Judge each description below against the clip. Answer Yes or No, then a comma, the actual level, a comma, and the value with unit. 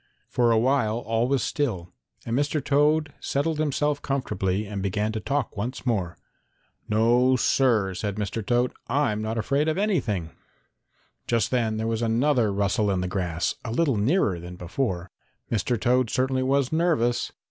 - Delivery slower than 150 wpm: No, average, 160 wpm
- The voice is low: Yes, low, 115 Hz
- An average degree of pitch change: Yes, average, 4.8 semitones